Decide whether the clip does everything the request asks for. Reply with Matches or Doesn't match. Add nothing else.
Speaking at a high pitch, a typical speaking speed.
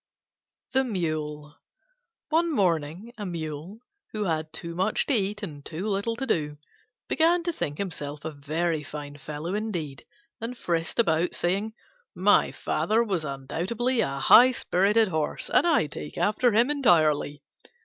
Doesn't match